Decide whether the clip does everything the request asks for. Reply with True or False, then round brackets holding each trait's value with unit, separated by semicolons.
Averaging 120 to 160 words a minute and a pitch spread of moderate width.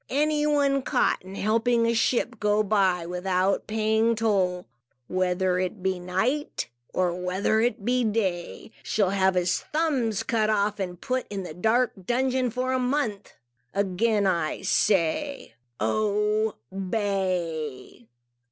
True (135 wpm; 4.2 semitones)